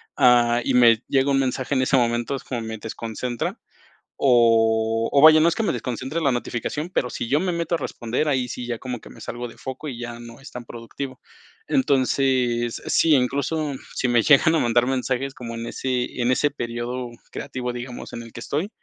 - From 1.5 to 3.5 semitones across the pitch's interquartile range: Yes, narrow, 2.5 semitones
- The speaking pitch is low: Yes, low, 125 Hz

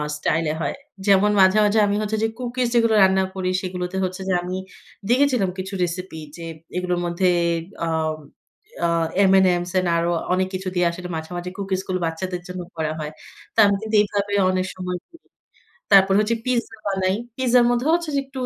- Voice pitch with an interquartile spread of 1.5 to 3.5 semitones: Yes, average, 3.1 semitones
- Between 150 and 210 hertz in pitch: Yes, high, 190 Hz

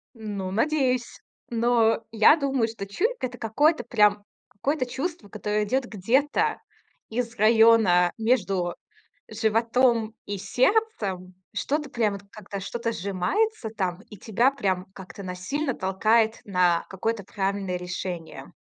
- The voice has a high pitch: Yes, high, 220 Hz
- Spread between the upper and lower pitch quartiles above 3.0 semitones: Yes, average, 4.3 semitones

